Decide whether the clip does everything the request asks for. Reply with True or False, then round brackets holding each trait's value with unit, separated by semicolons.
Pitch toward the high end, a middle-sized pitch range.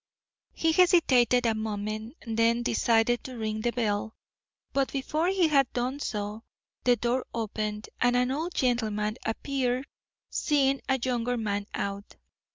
True (240 Hz; 3.5 semitones)